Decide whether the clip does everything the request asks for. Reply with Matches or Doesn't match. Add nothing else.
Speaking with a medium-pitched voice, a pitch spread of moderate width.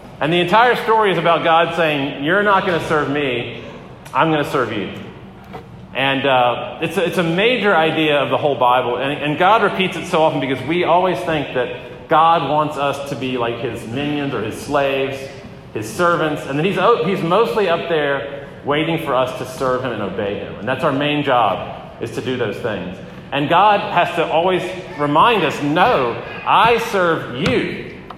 Matches